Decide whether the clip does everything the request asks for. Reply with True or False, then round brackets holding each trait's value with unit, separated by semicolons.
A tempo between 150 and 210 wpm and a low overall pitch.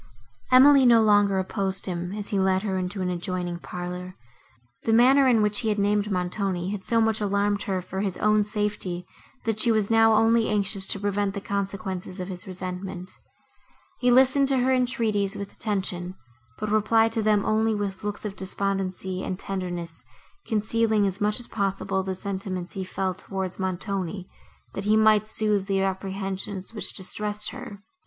False (175 wpm; 200 Hz)